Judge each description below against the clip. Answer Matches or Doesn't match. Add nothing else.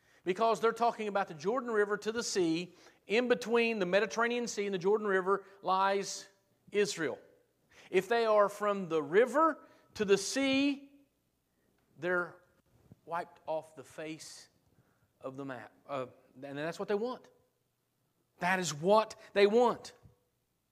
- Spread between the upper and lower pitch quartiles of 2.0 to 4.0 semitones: Doesn't match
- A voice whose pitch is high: Matches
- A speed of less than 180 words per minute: Matches